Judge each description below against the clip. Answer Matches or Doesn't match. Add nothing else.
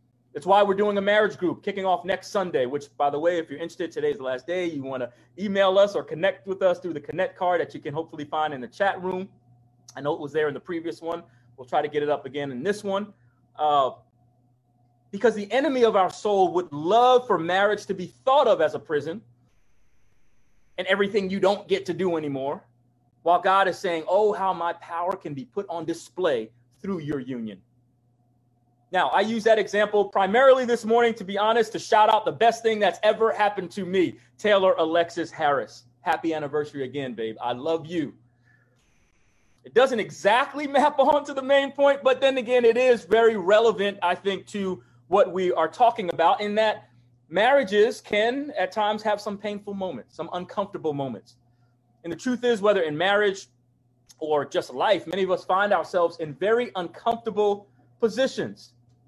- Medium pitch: Matches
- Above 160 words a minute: Matches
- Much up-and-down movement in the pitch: Matches